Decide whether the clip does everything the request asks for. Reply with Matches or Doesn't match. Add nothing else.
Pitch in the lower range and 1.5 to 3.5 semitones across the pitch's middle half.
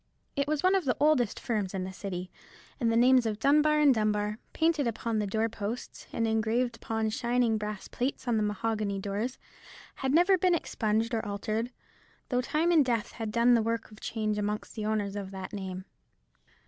Doesn't match